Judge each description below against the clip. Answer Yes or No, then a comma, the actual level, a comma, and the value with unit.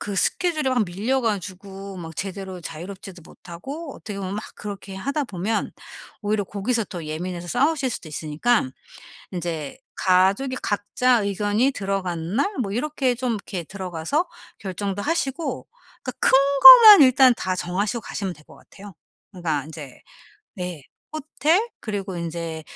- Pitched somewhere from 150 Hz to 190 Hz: No, high, 200 Hz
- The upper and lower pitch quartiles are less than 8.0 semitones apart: Yes, wide, 6.0 semitones